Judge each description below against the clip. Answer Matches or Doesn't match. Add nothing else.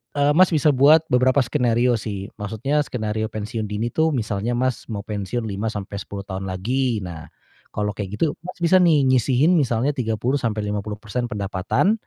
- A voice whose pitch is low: Matches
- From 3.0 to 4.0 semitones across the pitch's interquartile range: Doesn't match